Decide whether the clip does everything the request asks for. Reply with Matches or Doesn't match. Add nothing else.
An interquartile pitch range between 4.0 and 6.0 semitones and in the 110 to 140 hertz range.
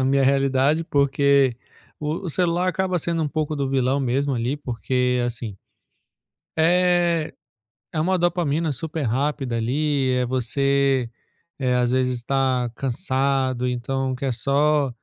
Doesn't match